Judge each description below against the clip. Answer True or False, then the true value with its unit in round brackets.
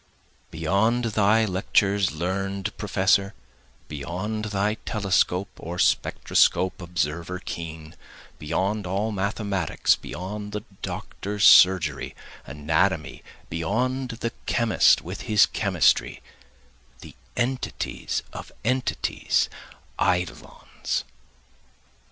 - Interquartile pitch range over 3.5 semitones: False (3.2 semitones)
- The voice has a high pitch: False (95 Hz)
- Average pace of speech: False (85 wpm)